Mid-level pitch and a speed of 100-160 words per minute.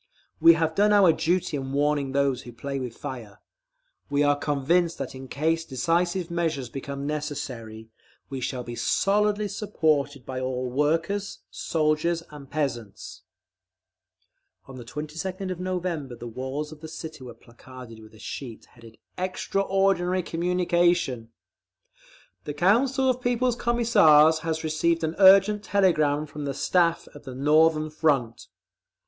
Yes: medium, 155 Hz; average, 140 wpm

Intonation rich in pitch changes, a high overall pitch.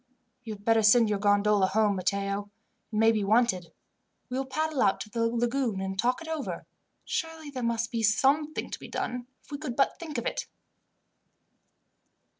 No: average, 4.4 semitones; high, 230 Hz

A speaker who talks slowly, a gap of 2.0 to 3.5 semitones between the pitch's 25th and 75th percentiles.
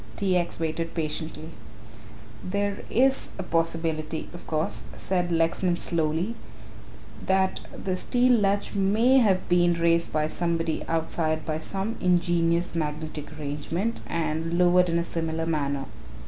Yes: slow, 130 wpm; average, 2.7 semitones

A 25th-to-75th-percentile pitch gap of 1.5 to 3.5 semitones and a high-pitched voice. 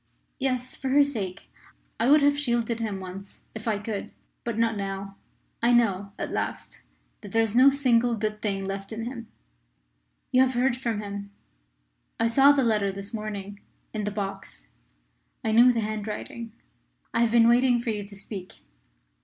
Yes: average, 3.1 semitones; high, 225 Hz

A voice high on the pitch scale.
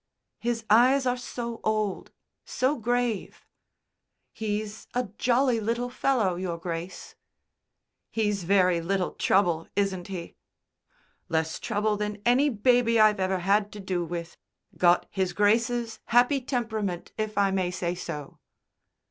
Yes: high, 210 Hz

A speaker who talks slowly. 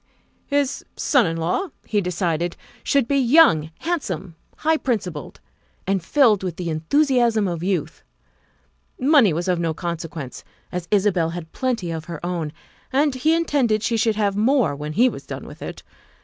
No: average, 165 wpm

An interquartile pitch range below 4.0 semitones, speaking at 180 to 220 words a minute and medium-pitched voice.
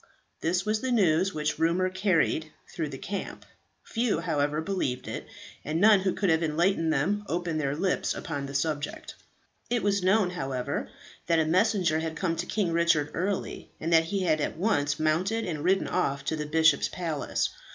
Yes: average, 3.6 semitones; average, 185 wpm; medium, 165 Hz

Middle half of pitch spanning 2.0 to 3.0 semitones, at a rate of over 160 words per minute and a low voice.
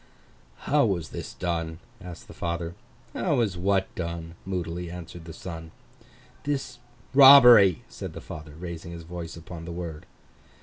No: narrow, 2.5 semitones; average, 145 wpm; very low, 85 Hz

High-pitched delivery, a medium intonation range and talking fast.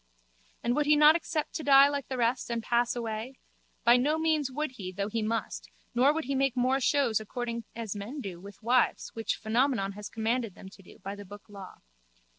Yes: high, 240 Hz; average, 4.1 semitones; fast, 215 wpm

